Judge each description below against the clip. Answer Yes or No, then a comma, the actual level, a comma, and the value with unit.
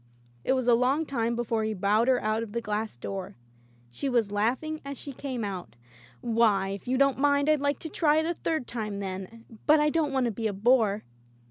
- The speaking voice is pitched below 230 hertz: No, high, 235 Hz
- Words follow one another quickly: Yes, fast, 225 wpm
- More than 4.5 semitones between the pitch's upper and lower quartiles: Yes, average, 4.9 semitones